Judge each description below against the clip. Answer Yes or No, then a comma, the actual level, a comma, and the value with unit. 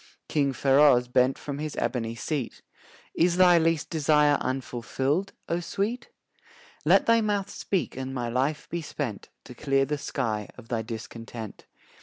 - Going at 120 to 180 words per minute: Yes, average, 150 wpm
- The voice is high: No, medium, 140 Hz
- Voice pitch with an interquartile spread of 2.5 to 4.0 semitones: No, average, 4.9 semitones